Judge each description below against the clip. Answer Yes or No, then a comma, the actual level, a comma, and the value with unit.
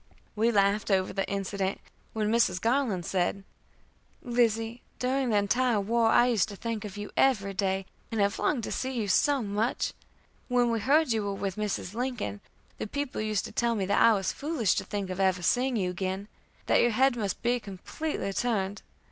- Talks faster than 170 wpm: Yes, average, 195 wpm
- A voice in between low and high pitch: No, high, 215 Hz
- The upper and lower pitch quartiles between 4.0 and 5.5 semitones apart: No, average, 3.5 semitones